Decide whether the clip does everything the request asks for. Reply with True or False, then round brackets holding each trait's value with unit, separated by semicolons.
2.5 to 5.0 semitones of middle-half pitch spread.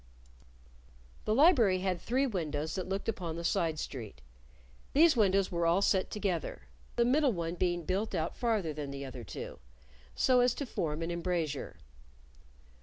False (5.5 semitones)